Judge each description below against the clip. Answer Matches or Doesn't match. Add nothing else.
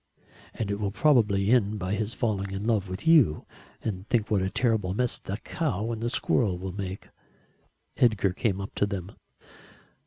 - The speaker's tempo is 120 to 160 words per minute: Doesn't match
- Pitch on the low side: Matches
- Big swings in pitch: Doesn't match